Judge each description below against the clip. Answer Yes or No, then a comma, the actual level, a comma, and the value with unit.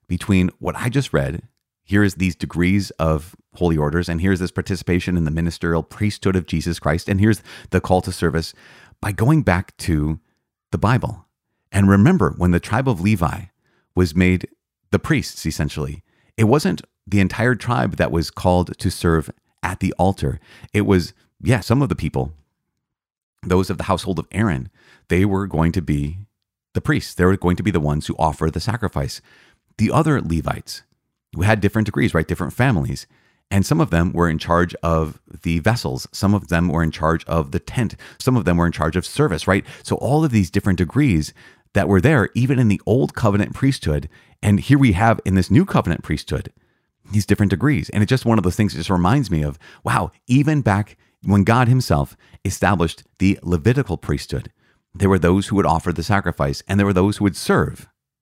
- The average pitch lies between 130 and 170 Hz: No, very low, 95 Hz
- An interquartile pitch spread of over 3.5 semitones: Yes, average, 4.1 semitones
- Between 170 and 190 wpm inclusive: No, average, 200 wpm